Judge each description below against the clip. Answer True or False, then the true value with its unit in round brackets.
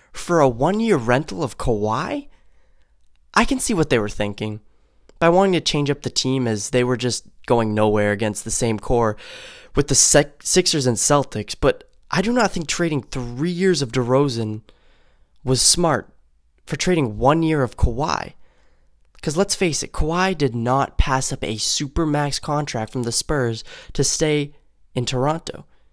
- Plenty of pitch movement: True (6.0 semitones)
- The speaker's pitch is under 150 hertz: True (135 Hz)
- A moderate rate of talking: True (175 wpm)